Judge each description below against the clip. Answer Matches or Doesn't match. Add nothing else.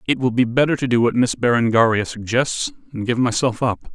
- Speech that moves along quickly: Matches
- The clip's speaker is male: Matches